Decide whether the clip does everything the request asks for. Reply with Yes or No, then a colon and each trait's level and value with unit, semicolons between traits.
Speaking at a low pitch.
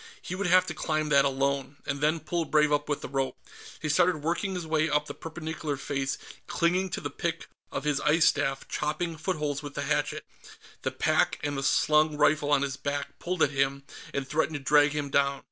No: medium, 150 Hz